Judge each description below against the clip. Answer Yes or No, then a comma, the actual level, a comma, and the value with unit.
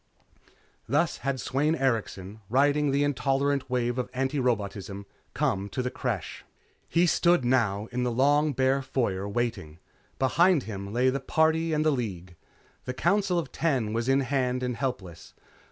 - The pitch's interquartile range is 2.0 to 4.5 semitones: Yes, average, 3.9 semitones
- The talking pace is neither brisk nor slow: Yes, average, 155 wpm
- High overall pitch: No, low, 130 Hz